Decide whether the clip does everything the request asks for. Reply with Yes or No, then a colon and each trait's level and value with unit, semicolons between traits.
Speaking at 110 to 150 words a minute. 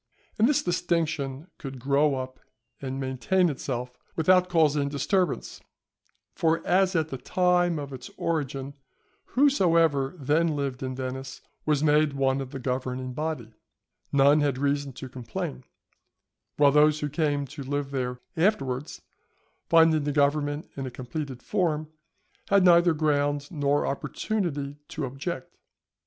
Yes: slow, 135 wpm